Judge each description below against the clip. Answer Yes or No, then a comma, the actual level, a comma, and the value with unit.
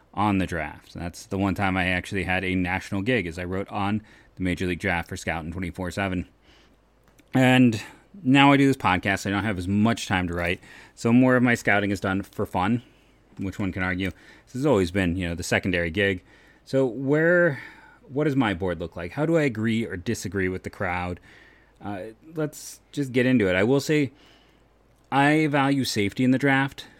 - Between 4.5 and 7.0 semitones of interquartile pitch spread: Yes, wide, 5.6 semitones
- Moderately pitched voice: No, low, 100 Hz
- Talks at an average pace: No, fast, 210 wpm